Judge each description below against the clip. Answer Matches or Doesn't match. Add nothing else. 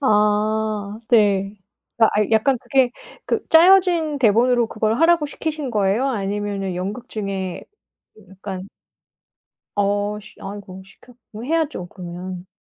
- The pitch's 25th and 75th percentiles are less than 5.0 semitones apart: Matches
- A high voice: Matches